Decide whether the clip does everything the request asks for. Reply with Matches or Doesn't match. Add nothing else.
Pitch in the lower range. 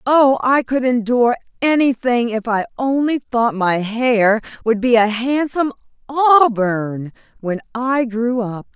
Doesn't match